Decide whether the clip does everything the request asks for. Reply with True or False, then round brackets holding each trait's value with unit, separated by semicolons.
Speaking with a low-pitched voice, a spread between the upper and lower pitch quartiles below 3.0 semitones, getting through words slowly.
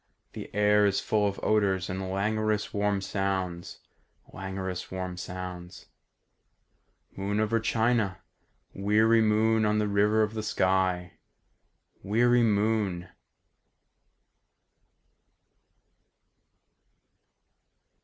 True (100 Hz; 2.4 semitones; 85 wpm)